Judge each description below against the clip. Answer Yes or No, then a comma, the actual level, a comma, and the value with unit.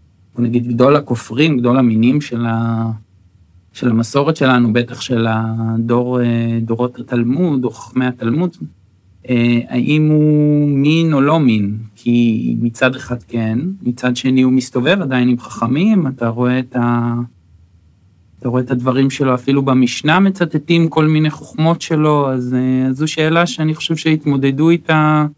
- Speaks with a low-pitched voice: Yes, low, 125 Hz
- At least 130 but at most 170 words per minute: Yes, average, 135 wpm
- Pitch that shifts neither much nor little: Yes, average, 4.3 semitones